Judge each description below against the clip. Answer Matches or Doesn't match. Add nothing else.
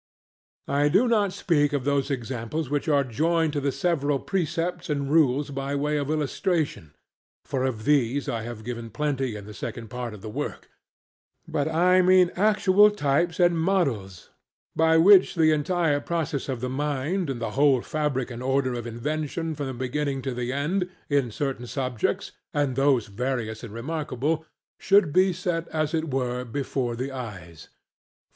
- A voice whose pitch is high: Doesn't match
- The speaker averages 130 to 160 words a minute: Doesn't match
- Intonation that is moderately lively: Matches